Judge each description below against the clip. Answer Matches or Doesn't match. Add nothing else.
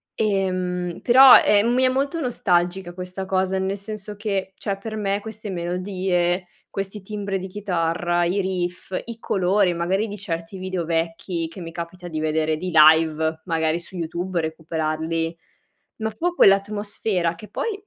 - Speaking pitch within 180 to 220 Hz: Matches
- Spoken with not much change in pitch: Doesn't match